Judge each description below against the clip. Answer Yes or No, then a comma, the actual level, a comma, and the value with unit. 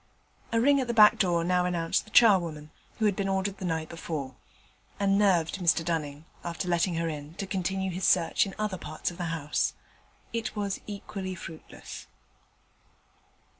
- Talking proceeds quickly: No, average, 170 wpm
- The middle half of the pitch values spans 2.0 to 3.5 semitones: Yes, average, 3.2 semitones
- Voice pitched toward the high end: No, medium, 180 Hz